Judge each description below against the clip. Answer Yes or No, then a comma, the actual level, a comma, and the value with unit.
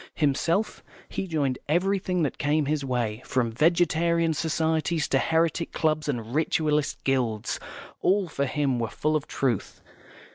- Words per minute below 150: Yes, average, 140 wpm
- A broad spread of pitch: No, average, 3.5 semitones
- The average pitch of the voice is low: No, medium, 155 Hz